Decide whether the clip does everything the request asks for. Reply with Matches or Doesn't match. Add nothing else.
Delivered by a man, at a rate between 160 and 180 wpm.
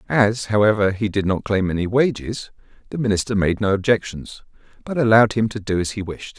Doesn't match